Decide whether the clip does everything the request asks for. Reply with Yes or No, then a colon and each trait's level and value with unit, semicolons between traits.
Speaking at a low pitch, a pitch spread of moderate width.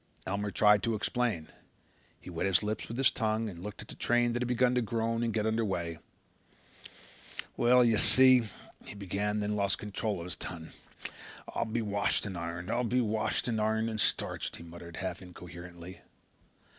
Yes: low, 105 Hz; average, 3.7 semitones